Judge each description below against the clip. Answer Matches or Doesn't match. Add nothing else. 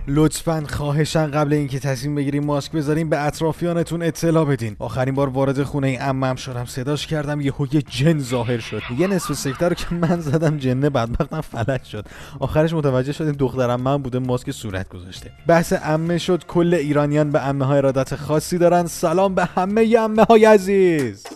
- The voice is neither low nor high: Matches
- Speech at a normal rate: Doesn't match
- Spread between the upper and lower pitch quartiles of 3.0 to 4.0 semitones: Matches